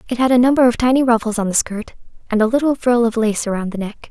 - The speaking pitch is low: No, high, 235 Hz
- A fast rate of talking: Yes, fast, 280 wpm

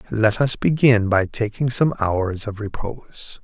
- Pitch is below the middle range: Yes, low, 110 Hz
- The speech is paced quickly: No, average, 155 wpm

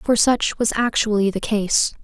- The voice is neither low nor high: No, high, 215 Hz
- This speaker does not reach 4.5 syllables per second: Yes, 4.2 syllables/s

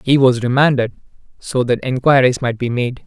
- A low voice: Yes, low, 125 Hz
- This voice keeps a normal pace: Yes, average, 175 wpm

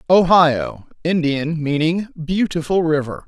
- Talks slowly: Yes, slow, 75 wpm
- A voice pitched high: No, medium, 160 Hz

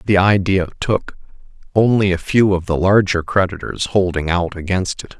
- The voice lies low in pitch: Yes, very low, 95 Hz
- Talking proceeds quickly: No, average, 160 wpm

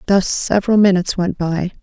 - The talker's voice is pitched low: No, medium, 185 Hz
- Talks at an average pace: Yes, average, 165 wpm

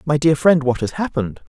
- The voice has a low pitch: No, medium, 145 Hz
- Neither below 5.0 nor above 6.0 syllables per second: Yes, 5.8 syllables/s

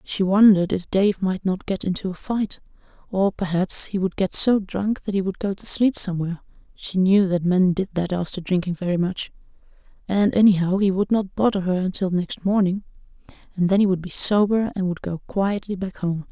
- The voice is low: No, high, 190 Hz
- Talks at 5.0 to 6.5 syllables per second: Yes, 5.3 syllables/s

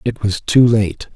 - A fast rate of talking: Yes, fast, 210 wpm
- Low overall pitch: Yes, low, 110 Hz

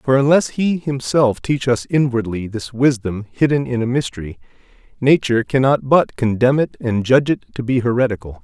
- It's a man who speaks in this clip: Yes, male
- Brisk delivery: No, average, 170 wpm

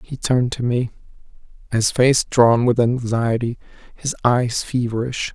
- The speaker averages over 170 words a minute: No, slow, 135 wpm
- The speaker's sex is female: No, male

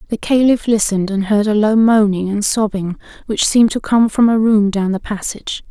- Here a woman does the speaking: Yes, female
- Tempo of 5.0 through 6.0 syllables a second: Yes, 5.4 syllables/s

